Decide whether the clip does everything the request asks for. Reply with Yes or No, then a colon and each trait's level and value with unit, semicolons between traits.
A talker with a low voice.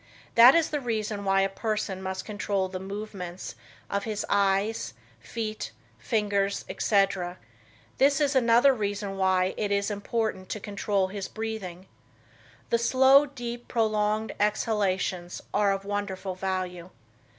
No: high, 205 Hz